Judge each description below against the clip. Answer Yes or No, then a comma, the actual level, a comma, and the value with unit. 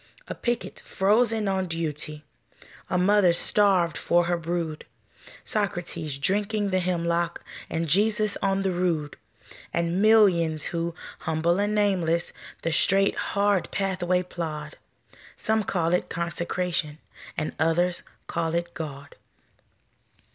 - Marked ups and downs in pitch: No, average, 3.0 semitones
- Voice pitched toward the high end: No, medium, 175 Hz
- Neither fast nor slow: No, slow, 120 wpm